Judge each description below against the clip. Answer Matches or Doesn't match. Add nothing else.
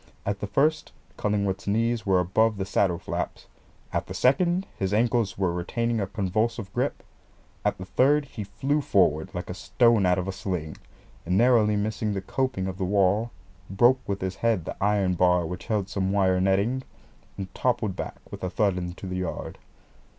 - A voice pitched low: Matches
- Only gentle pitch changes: Doesn't match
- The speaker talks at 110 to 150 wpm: Doesn't match